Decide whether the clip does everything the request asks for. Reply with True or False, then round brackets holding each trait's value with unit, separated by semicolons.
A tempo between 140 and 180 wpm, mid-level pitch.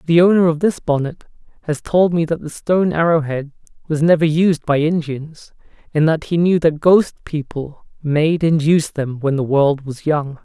False (195 wpm; 155 Hz)